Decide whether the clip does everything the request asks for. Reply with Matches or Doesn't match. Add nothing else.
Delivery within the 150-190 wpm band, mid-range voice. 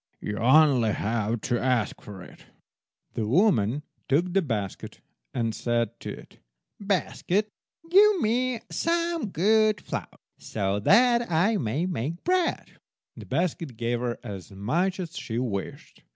Doesn't match